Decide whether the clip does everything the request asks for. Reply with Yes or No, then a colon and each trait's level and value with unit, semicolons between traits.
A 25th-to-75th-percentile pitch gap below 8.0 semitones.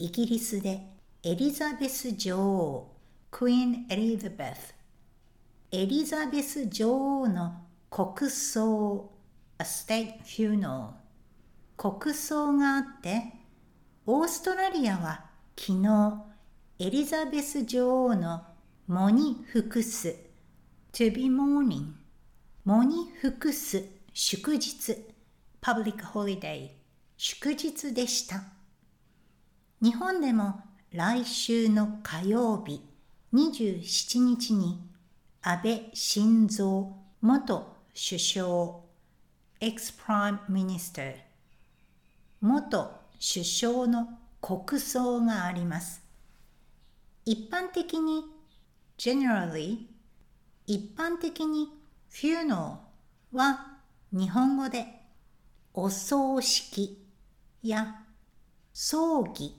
Yes: wide, 5.6 semitones